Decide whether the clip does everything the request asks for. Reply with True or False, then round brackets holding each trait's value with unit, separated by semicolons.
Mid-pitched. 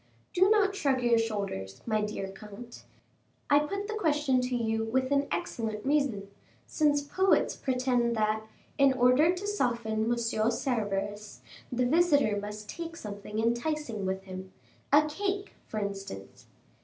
False (240 Hz)